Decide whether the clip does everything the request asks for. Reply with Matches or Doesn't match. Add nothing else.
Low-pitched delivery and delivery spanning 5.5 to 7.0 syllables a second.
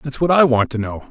Matches